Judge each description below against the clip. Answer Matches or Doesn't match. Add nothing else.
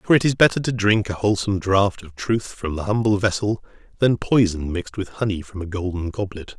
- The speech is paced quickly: Matches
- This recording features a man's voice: Matches